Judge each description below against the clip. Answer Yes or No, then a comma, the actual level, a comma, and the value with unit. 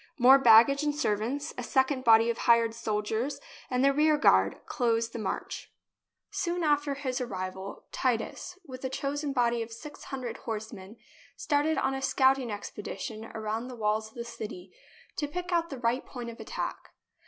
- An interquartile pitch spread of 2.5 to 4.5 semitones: Yes, average, 3.8 semitones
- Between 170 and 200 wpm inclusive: Yes, average, 175 wpm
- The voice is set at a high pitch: Yes, high, 245 Hz